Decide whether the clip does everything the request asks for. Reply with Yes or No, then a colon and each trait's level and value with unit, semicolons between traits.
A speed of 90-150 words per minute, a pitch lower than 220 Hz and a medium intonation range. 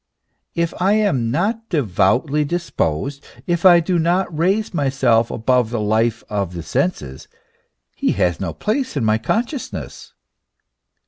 No: average, 140 wpm; medium, 140 Hz; wide, 8.1 semitones